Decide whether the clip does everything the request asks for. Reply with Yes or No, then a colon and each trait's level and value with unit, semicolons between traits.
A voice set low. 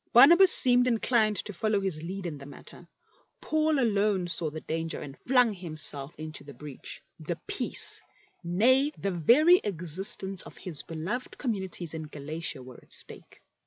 No: high, 190 Hz